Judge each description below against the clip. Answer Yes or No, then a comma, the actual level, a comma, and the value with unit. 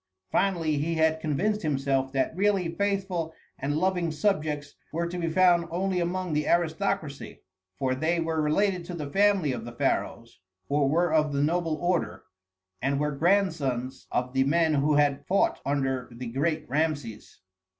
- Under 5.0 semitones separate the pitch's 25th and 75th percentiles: Yes, average, 3.8 semitones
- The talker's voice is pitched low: No, medium, 155 Hz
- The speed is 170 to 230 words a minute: No, average, 160 wpm